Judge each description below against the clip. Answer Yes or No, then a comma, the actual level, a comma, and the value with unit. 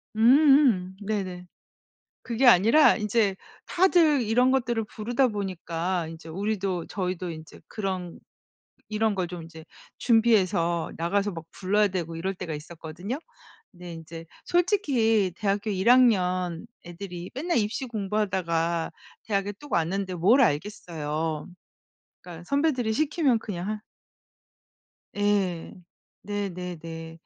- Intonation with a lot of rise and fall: No, average, 4.6 semitones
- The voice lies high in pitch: Yes, high, 195 Hz